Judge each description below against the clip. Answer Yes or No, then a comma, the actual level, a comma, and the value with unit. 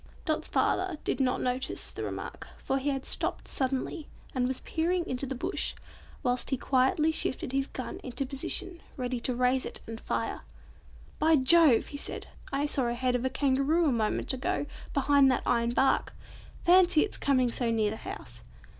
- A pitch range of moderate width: Yes, average, 3.3 semitones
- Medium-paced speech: Yes, average, 180 wpm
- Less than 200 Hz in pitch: No, very high, 265 Hz